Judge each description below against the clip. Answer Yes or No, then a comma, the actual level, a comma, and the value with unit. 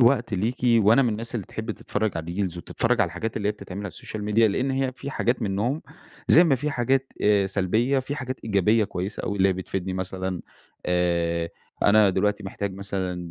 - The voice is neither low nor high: No, low, 105 Hz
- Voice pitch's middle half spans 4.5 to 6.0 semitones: No, average, 4.1 semitones